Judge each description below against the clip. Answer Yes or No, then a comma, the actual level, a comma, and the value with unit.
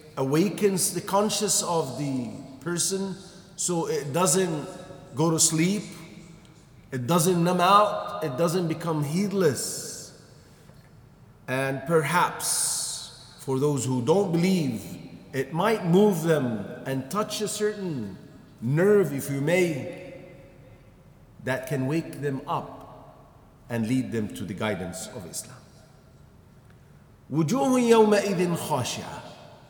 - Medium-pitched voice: Yes, medium, 165 Hz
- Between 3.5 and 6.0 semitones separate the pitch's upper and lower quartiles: Yes, average, 5.3 semitones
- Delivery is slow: Yes, slow, 105 wpm